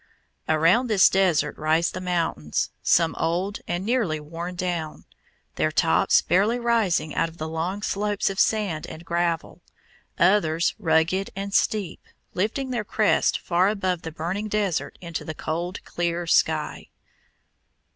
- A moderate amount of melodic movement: Yes, average, 3.6 semitones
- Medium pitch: Yes, medium, 175 Hz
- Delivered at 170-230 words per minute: No, average, 140 wpm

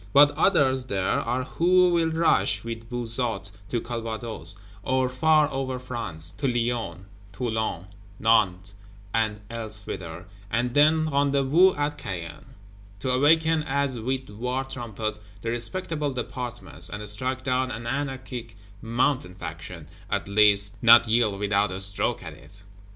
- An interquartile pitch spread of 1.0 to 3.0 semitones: No, average, 4.2 semitones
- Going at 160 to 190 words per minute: No, slow, 135 wpm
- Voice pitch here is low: Yes, low, 120 Hz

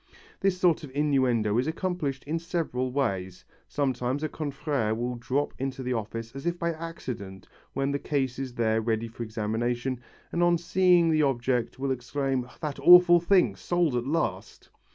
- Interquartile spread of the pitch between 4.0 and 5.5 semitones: Yes, average, 5.2 semitones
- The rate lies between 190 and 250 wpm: No, average, 170 wpm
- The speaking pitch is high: No, low, 135 Hz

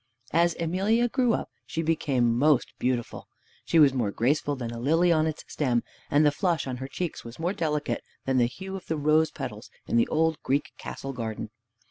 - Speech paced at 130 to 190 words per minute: No, average, 200 wpm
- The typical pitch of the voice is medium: Yes, medium, 150 Hz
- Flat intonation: No, average, 4.6 semitones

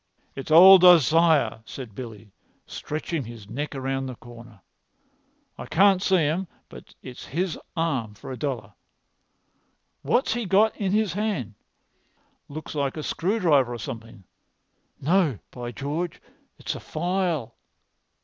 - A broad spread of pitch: Yes, wide, 6.9 semitones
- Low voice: No, medium, 150 Hz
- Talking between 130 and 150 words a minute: Yes, slow, 135 wpm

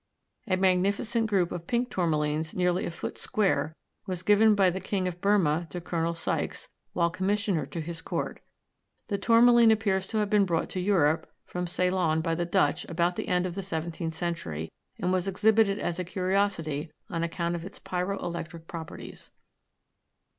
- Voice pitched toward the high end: No, medium, 180 Hz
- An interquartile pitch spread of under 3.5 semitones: Yes, average, 2.9 semitones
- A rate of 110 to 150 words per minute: No, average, 175 wpm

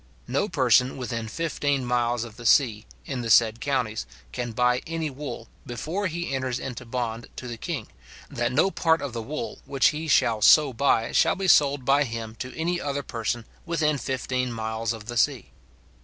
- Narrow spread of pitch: No, average, 3.8 semitones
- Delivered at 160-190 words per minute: Yes, average, 185 wpm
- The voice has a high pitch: No, low, 125 Hz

